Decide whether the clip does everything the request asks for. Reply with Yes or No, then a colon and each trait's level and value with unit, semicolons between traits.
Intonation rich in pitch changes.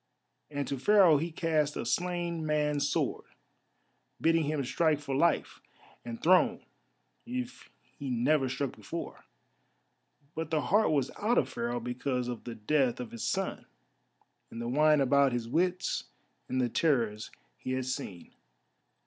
No: average, 4.7 semitones